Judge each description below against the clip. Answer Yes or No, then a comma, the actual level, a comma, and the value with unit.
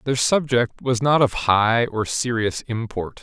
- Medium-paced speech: Yes, average, 170 wpm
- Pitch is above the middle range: No, low, 120 Hz